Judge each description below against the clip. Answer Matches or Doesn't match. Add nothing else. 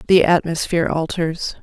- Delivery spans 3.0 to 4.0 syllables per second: Doesn't match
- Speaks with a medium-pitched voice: Matches